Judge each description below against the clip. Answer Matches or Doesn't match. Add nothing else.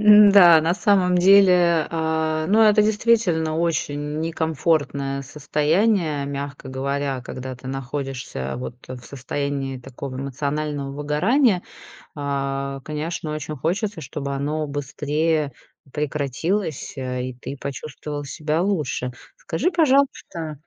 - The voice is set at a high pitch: Doesn't match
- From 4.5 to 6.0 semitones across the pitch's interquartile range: Doesn't match